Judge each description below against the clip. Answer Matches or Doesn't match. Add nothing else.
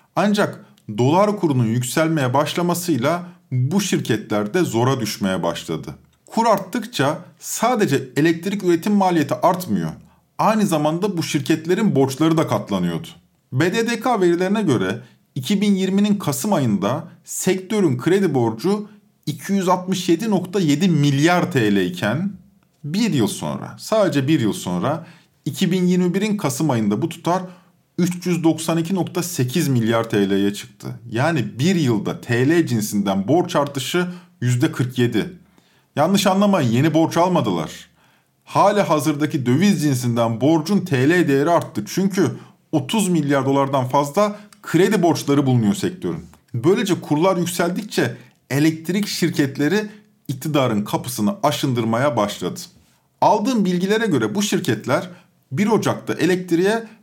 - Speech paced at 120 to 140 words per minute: Doesn't match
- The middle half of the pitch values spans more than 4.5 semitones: Matches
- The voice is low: Doesn't match